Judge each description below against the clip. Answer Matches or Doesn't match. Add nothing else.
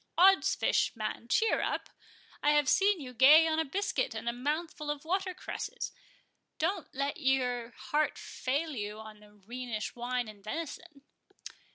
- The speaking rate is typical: Matches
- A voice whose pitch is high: Matches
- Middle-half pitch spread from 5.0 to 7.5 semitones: Matches